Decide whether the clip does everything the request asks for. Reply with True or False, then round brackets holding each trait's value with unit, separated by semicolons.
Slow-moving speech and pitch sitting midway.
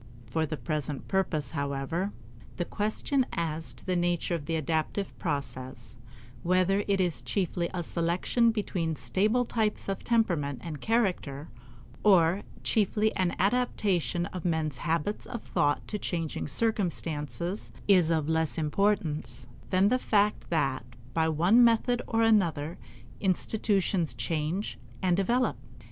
True (130 wpm; 175 Hz)